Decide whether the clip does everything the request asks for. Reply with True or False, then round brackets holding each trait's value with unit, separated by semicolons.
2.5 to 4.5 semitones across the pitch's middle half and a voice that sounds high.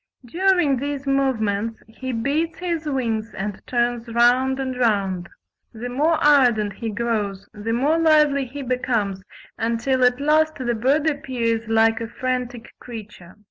True (3.7 semitones; 245 Hz)